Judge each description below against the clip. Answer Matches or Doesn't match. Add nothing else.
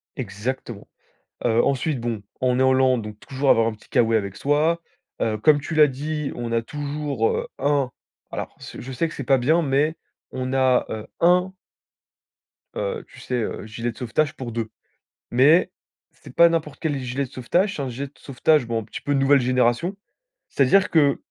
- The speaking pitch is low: Matches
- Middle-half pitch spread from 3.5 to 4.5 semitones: Matches